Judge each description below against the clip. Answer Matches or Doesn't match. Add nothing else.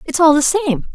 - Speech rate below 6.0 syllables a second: Matches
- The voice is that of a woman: Matches